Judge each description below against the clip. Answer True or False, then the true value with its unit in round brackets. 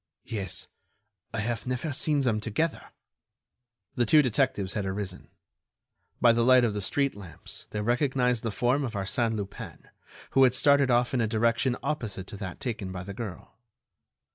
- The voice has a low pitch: True (115 Hz)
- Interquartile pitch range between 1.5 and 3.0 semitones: False (3.9 semitones)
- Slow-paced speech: False (165 wpm)